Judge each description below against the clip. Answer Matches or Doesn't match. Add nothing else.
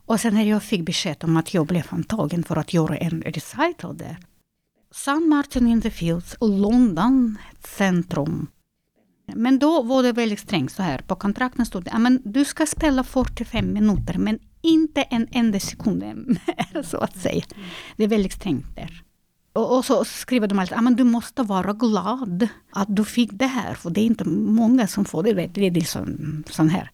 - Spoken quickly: Doesn't match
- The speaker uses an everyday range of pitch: Doesn't match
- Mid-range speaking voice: Doesn't match